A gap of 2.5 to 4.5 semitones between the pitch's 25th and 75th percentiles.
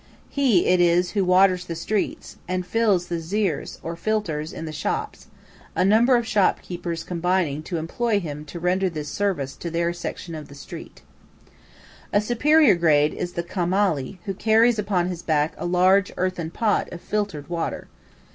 Yes: average, 3.5 semitones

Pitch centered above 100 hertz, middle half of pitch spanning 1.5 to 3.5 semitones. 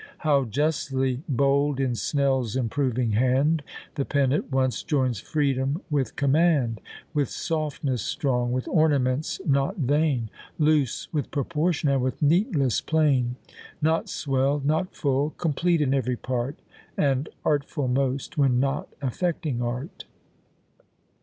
Yes: medium, 140 Hz; average, 2.8 semitones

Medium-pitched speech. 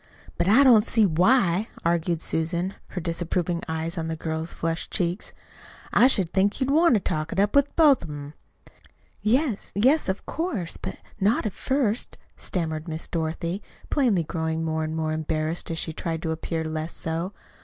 Yes: medium, 170 Hz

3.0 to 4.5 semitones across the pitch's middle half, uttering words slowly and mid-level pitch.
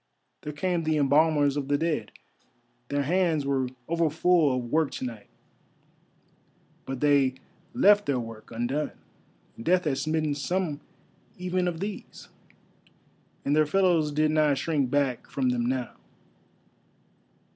Yes: average, 3.5 semitones; slow, 130 wpm; medium, 150 Hz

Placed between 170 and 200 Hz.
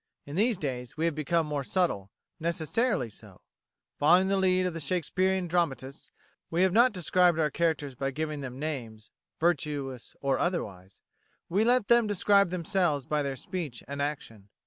No: medium, 160 Hz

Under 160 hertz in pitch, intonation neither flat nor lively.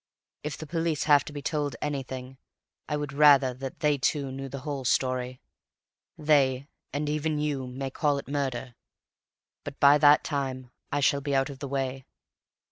No: medium, 140 Hz; narrow, 2.0 semitones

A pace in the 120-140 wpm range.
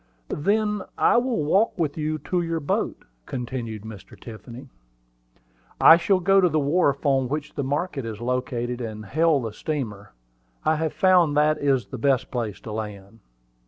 No: average, 165 wpm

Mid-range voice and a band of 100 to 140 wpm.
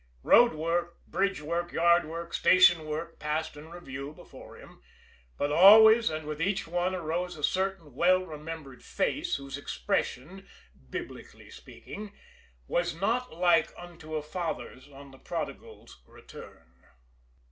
Yes: medium, 165 Hz; slow, 135 wpm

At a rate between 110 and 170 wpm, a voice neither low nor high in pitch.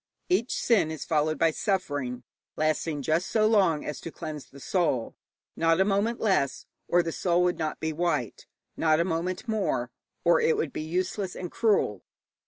No: average, 180 wpm; medium, 170 Hz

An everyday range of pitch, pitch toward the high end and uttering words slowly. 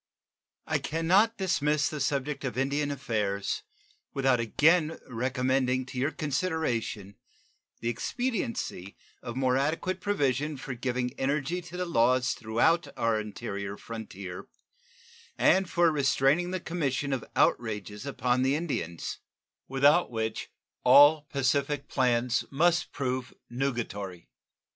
No: average, 4.3 semitones; low, 135 Hz; slow, 120 wpm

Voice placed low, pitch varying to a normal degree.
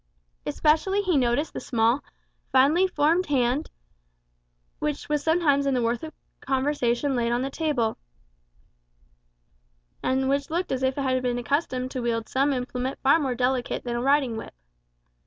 No: very high, 265 Hz; average, 3.1 semitones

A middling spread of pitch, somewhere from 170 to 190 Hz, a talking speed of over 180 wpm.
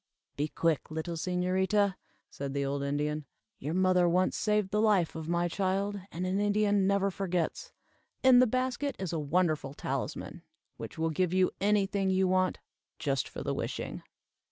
No: average, 3.7 semitones; medium, 185 Hz; average, 170 wpm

